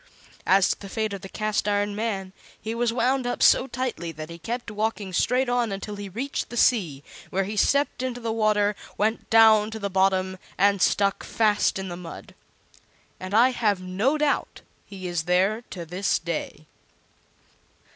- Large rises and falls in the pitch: No, average, 3.3 semitones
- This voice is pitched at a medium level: No, high, 205 Hz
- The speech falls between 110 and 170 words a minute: No, average, 180 wpm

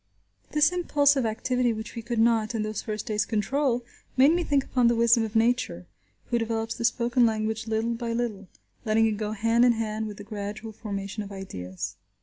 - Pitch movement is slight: Yes, narrow, 2.0 semitones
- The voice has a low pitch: No, high, 225 Hz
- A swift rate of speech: No, average, 195 wpm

